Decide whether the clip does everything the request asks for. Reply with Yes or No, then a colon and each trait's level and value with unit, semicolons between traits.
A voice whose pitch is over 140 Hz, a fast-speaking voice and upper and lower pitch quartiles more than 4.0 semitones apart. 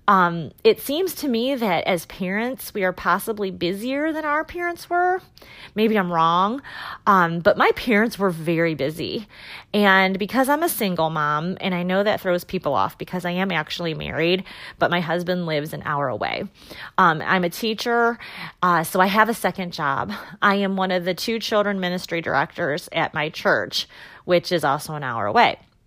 No: medium, 185 Hz; average, 185 wpm; average, 4.6 semitones